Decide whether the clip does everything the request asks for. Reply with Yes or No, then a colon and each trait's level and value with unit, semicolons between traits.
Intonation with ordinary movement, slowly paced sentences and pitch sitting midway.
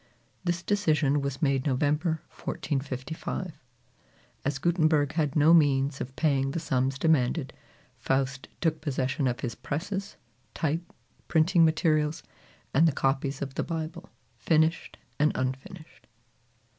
Yes: average, 3.1 semitones; slow, 120 wpm; medium, 150 Hz